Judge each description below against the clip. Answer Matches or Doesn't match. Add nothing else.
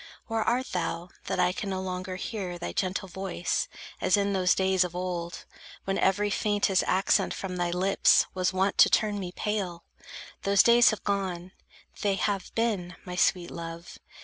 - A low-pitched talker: Doesn't match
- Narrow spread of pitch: Matches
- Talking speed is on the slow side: Doesn't match